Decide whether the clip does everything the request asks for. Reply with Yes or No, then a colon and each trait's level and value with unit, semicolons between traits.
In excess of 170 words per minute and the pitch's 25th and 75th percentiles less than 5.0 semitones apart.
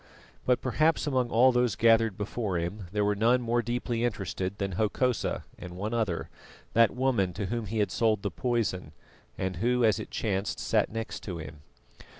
Yes: average, 180 wpm; average, 3.6 semitones